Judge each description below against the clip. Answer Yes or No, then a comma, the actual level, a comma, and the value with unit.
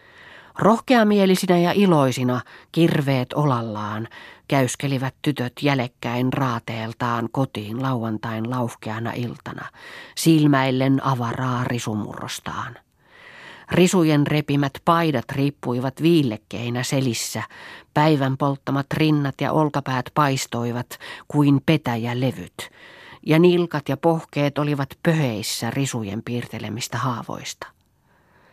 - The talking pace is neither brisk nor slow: No, slow, 85 wpm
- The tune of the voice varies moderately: Yes, average, 3.9 semitones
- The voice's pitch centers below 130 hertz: No, low, 135 Hz